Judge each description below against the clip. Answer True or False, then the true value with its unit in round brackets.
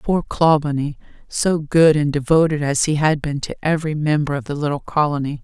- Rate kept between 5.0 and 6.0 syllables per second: True (5.4 syllables/s)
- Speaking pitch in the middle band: True (150 Hz)